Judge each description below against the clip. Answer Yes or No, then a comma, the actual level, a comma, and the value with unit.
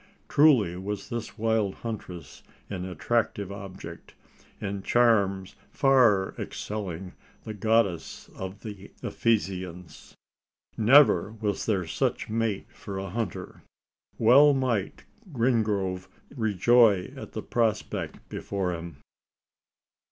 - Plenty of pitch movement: No, average, 3.4 semitones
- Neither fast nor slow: No, slow, 100 wpm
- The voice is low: Yes, low, 105 Hz